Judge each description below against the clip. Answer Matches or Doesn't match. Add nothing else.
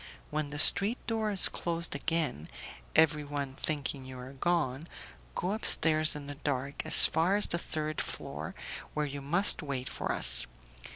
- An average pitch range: Matches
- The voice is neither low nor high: Matches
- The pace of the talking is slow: Doesn't match